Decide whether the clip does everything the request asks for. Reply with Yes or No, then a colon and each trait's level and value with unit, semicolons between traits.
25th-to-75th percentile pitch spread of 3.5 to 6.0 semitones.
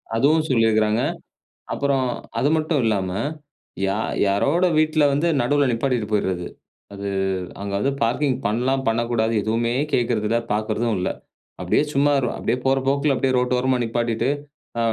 Yes: average, 3.9 semitones